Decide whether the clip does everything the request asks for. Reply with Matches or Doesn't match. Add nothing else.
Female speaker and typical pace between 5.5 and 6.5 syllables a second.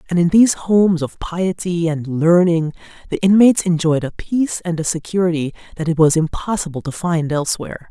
Matches